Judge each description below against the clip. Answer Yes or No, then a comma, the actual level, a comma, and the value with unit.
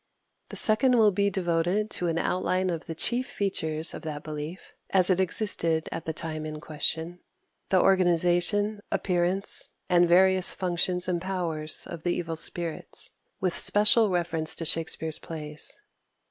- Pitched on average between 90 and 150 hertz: No, medium, 175 Hz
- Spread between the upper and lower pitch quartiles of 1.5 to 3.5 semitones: Yes, average, 2.7 semitones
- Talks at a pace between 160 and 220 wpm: No, average, 150 wpm